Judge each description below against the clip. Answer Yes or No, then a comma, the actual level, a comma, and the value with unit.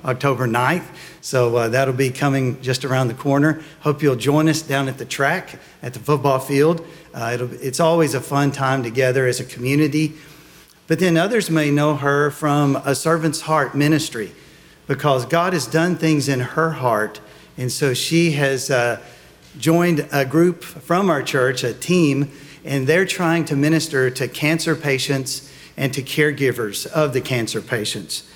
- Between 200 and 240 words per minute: No, average, 170 wpm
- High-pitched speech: No, medium, 140 Hz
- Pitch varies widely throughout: No, average, 3.5 semitones